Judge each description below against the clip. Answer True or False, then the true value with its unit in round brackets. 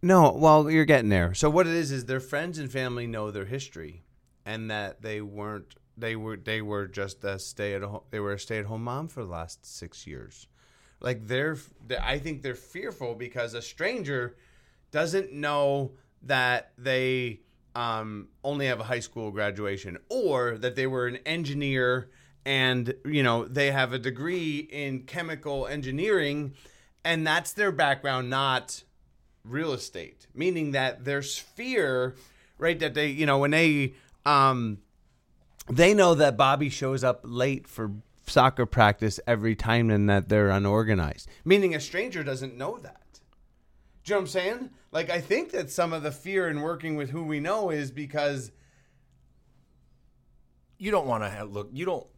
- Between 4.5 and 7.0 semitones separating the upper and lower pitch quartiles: True (5.1 semitones)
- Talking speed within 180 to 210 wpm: False (165 wpm)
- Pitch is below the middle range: True (130 Hz)